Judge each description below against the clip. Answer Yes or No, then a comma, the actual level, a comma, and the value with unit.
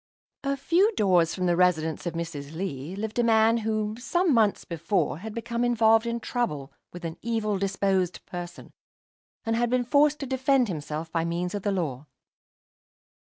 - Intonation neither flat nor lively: No, wide, 5.7 semitones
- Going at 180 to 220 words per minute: No, average, 165 wpm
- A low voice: No, high, 205 Hz